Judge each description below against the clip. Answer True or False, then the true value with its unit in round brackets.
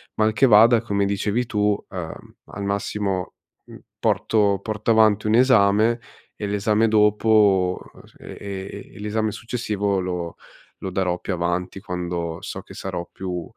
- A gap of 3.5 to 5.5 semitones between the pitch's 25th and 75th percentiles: False (2.7 semitones)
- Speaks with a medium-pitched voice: False (100 Hz)